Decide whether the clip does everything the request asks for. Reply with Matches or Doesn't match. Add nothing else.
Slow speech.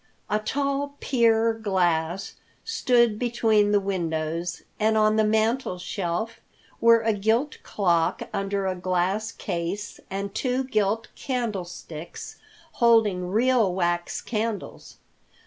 Matches